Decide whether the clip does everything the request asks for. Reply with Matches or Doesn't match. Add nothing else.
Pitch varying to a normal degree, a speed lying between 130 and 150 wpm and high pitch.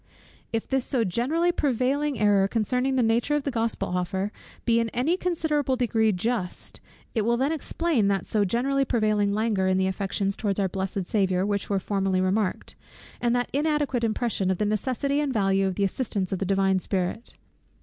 Doesn't match